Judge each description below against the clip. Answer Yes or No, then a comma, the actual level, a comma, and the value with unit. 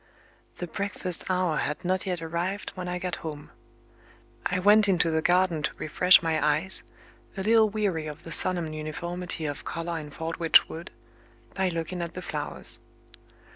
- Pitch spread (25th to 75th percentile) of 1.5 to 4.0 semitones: Yes, narrow, 2.5 semitones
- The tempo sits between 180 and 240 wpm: No, average, 165 wpm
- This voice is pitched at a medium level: Yes, medium, 175 Hz